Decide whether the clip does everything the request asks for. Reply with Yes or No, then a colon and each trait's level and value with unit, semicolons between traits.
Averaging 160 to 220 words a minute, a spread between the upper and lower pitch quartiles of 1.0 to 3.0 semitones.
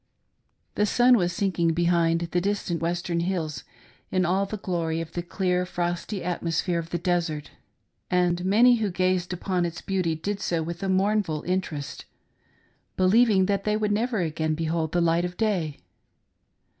Yes: average, 170 wpm; narrow, 2.5 semitones